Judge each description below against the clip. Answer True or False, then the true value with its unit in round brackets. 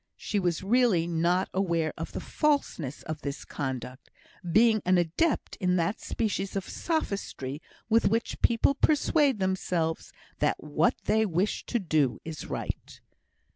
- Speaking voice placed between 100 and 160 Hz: False (185 Hz)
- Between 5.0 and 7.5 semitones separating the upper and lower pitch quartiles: True (5.5 semitones)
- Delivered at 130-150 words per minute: True (140 wpm)